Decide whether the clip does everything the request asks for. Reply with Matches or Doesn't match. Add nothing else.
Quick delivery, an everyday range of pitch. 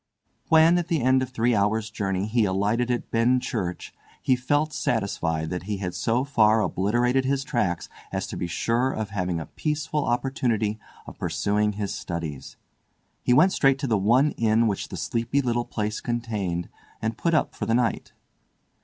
Doesn't match